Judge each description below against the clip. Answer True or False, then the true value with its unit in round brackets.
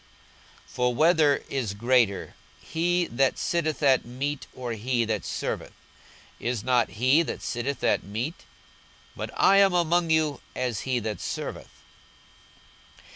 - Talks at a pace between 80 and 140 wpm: True (135 wpm)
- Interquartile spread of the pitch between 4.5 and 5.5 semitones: True (5.0 semitones)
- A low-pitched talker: True (130 Hz)